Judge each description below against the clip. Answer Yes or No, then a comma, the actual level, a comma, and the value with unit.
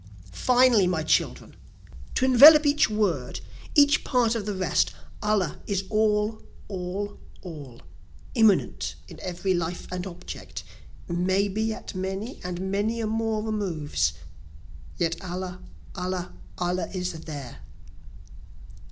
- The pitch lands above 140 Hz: Yes, high, 190 Hz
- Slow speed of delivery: Yes, slow, 120 wpm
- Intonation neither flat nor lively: Yes, average, 3.5 semitones